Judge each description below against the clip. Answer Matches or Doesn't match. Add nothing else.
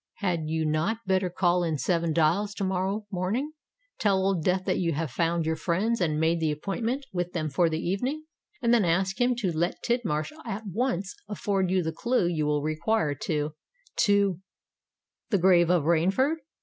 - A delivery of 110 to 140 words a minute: Doesn't match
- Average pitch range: Matches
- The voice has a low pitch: Doesn't match